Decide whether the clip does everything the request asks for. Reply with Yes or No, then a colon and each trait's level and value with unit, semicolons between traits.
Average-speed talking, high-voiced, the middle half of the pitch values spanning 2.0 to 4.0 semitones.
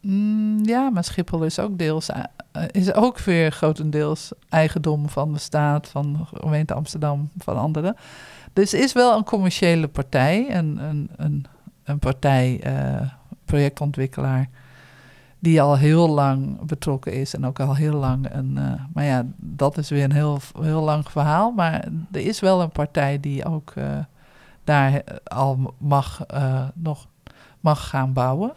No: average, 155 wpm; medium, 150 Hz; average, 3.4 semitones